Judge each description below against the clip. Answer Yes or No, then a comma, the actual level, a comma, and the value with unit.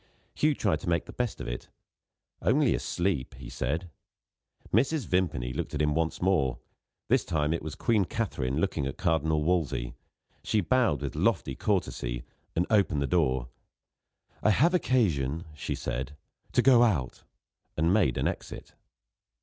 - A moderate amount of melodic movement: No, wide, 6.4 semitones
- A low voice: Yes, very low, 80 Hz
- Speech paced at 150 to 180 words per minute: Yes, average, 155 wpm